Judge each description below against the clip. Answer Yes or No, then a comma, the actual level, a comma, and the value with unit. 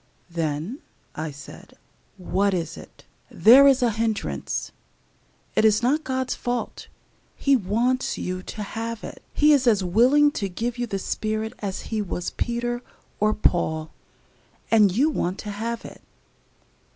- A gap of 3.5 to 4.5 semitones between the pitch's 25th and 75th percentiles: Yes, average, 4.2 semitones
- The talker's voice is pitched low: No, high, 220 Hz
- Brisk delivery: No, average, 150 wpm